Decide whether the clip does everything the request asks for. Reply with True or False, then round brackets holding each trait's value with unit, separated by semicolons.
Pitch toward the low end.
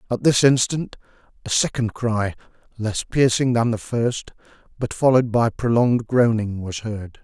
True (115 Hz)